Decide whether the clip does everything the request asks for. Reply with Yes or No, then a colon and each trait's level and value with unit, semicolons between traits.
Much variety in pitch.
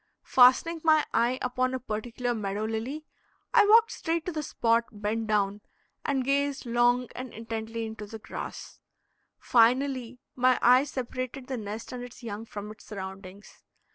No: average, 2.9 semitones